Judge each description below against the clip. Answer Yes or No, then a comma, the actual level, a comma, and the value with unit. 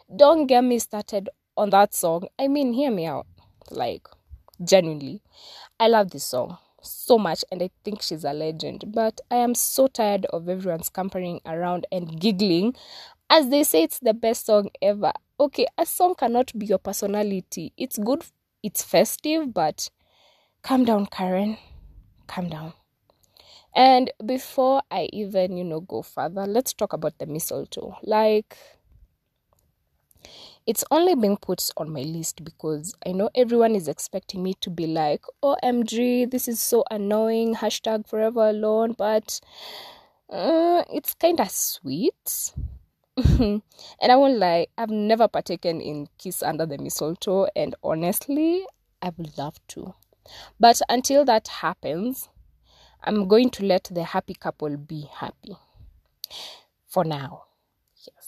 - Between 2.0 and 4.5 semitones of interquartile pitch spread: No, wide, 5.6 semitones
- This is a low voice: No, high, 210 Hz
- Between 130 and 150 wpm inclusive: Yes, average, 145 wpm